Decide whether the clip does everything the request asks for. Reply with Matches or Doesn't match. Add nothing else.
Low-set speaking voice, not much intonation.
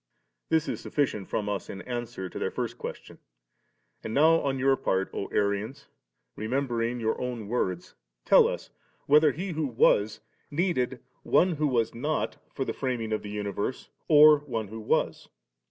Doesn't match